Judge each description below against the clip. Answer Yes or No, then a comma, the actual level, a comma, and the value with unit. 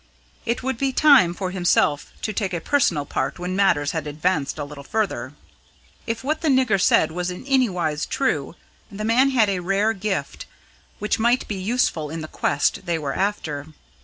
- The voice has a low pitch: No, high, 190 Hz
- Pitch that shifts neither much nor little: No, wide, 6.3 semitones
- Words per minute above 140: Yes, average, 190 wpm